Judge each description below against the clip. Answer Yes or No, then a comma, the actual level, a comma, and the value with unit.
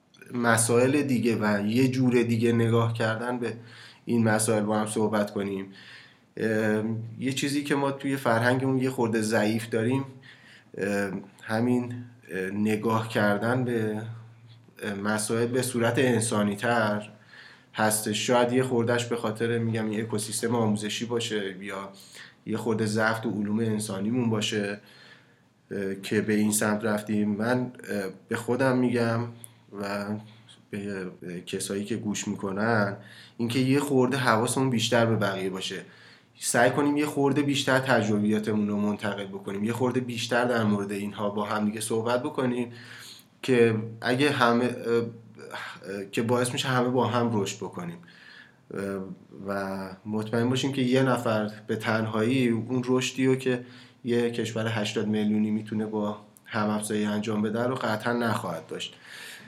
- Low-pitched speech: Yes, low, 115 Hz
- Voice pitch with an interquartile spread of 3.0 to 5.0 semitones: No, narrow, 2.5 semitones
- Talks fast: No, average, 135 wpm